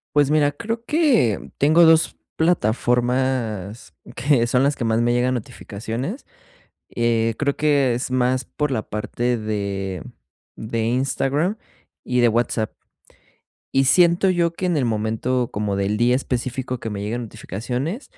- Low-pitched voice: Yes, low, 125 Hz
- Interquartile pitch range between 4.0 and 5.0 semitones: Yes, average, 4.3 semitones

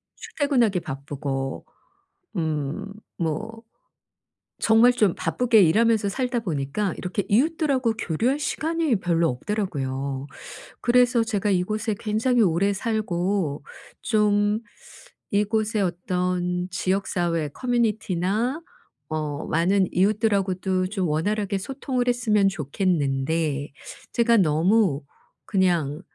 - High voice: Yes, high, 195 Hz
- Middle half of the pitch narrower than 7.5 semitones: Yes, average, 5.2 semitones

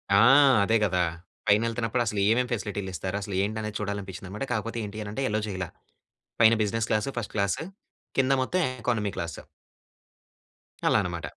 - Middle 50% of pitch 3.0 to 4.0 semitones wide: No, narrow, 2.5 semitones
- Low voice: Yes, low, 105 Hz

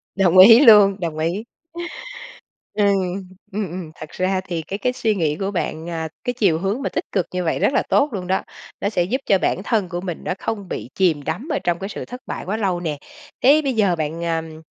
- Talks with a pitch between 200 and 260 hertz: No, high, 190 Hz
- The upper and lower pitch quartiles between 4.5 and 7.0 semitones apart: No, average, 3.8 semitones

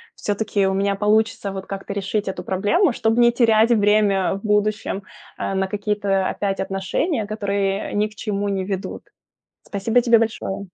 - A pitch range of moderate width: No, narrow, 1.8 semitones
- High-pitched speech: Yes, high, 205 Hz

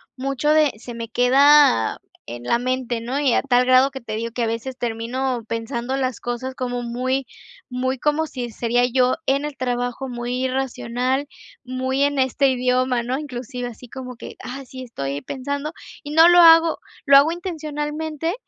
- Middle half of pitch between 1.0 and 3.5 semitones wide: Yes, narrow, 2.4 semitones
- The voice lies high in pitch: Yes, very high, 255 Hz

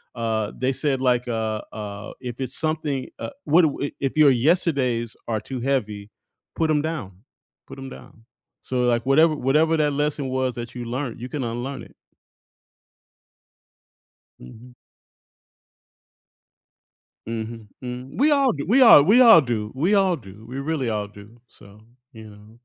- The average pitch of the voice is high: No, low, 130 Hz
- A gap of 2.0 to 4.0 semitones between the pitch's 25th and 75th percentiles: No, average, 4.6 semitones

